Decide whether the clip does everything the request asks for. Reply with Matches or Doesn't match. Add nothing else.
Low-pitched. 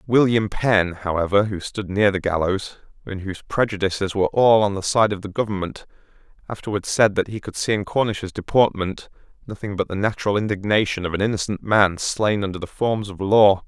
Matches